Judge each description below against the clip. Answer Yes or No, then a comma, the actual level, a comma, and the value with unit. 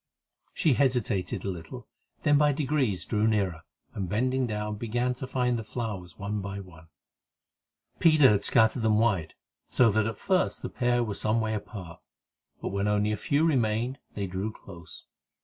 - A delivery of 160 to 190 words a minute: Yes, average, 170 wpm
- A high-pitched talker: No, low, 110 Hz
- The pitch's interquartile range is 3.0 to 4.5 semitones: Yes, average, 3.9 semitones